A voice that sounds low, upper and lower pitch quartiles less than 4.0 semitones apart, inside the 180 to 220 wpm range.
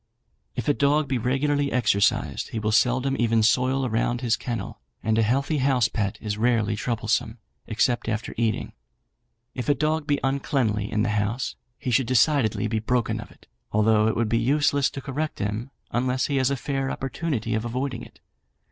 Yes: low, 120 Hz; average, 3.6 semitones; average, 185 wpm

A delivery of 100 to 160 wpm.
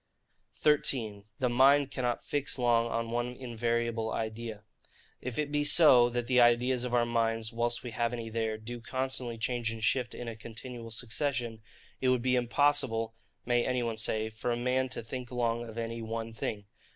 No: average, 185 wpm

